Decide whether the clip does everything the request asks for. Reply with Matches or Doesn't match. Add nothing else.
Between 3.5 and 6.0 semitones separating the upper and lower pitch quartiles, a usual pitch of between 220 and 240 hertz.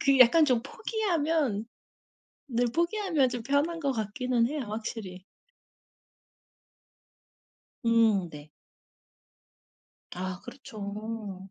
Matches